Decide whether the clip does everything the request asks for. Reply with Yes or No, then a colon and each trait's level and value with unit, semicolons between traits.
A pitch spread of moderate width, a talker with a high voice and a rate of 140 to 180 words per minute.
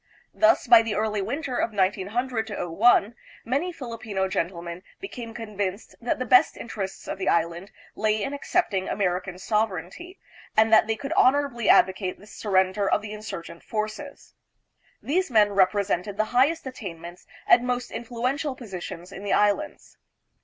Yes: average, 4.4 semitones; high, 215 Hz; average, 155 wpm